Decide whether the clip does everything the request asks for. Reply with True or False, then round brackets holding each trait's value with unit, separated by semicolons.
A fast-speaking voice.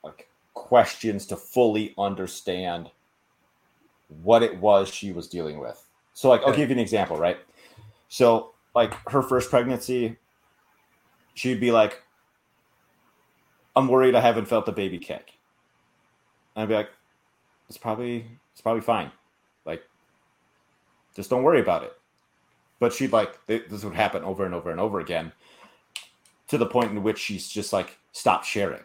False (150 wpm)